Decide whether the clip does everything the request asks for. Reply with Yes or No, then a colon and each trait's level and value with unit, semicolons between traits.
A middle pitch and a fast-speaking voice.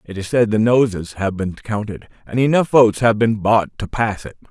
No: low, 110 Hz; fast, 225 wpm